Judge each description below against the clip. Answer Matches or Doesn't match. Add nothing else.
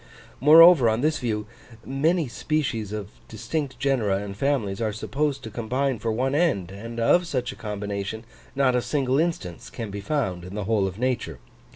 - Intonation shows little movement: Doesn't match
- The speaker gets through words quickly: Doesn't match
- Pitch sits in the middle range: Doesn't match